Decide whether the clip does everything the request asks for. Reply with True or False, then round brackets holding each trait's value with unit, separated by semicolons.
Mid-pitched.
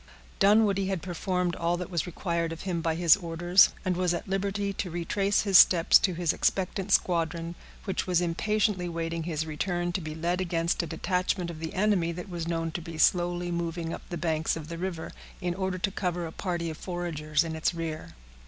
True (175 Hz)